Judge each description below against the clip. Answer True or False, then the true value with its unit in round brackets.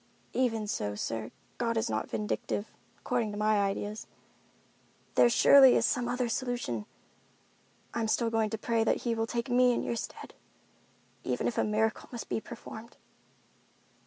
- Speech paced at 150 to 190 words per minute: True (160 wpm)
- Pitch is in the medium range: False (225 Hz)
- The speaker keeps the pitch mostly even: True (2.1 semitones)